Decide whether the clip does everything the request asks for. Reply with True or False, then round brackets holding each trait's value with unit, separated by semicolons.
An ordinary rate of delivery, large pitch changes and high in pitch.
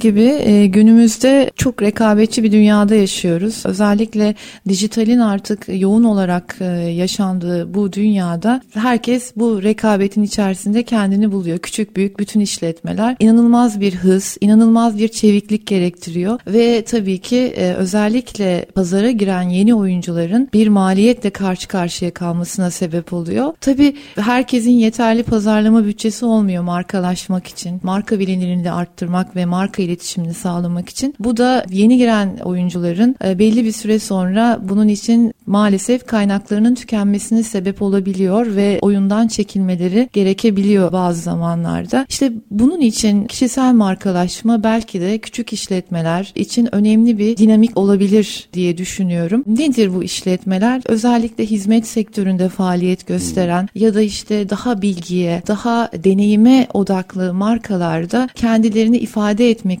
False (125 wpm; 3.4 semitones; 210 Hz)